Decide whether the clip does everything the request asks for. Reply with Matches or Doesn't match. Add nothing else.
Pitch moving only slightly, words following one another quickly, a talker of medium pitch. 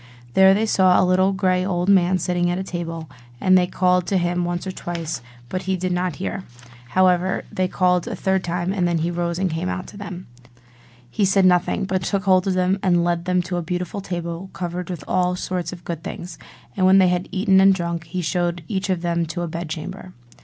Matches